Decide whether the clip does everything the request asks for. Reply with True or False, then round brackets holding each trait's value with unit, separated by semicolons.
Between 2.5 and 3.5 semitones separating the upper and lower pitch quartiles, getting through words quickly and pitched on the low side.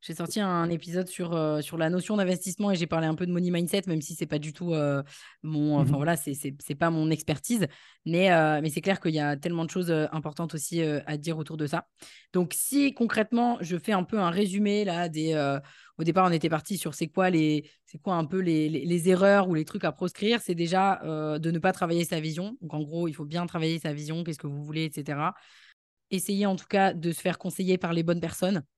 False (3.0 semitones; 255 wpm; 170 Hz)